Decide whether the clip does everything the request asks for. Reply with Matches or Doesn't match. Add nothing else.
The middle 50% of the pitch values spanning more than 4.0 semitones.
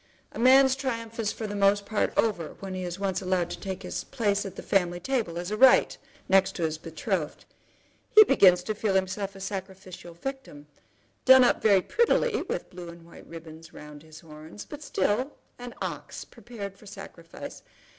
Matches